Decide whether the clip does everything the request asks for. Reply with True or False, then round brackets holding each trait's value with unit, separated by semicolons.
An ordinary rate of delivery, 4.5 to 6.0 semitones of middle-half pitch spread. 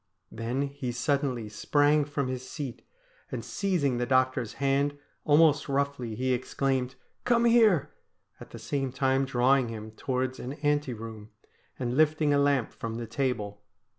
False (165 wpm; 2.9 semitones)